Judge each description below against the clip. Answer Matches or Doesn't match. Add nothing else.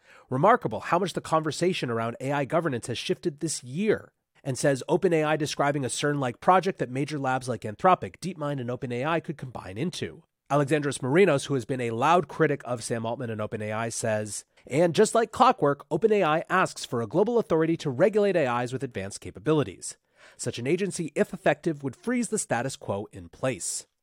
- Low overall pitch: Doesn't match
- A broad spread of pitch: Matches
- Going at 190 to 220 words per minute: Doesn't match